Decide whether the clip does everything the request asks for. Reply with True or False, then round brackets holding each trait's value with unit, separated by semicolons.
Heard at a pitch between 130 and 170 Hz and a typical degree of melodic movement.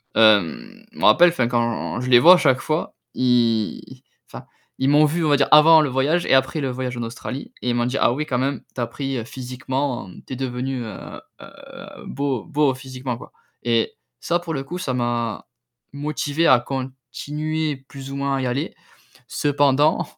True (135 Hz; 3.1 semitones)